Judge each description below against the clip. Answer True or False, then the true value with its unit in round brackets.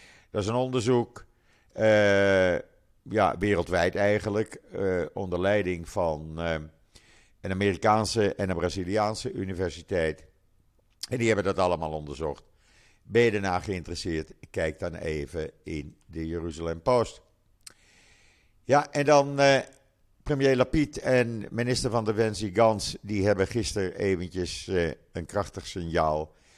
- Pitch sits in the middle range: False (100 Hz)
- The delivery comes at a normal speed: False (120 wpm)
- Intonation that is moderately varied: True (3.8 semitones)